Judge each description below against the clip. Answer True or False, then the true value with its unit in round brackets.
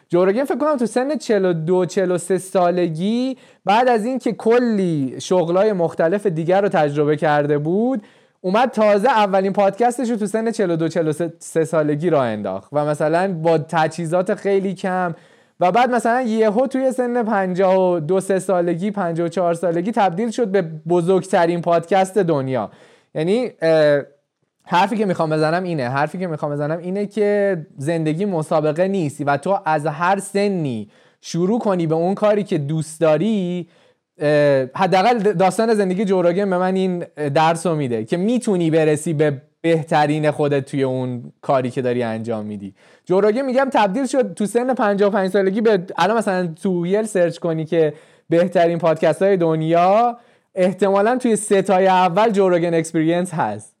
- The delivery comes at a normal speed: True (145 wpm)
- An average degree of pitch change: True (4.3 semitones)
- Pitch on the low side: False (180 Hz)